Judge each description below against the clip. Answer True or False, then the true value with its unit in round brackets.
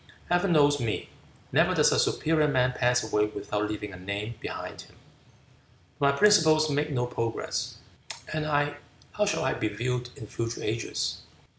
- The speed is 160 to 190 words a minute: True (165 wpm)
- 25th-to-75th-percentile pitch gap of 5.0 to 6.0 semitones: True (5.4 semitones)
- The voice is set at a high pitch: False (125 Hz)